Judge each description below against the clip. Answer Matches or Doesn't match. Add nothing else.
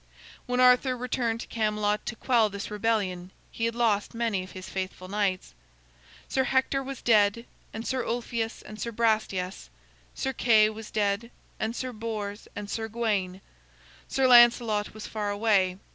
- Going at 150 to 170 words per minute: Matches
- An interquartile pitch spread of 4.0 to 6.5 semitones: Doesn't match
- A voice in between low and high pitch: Doesn't match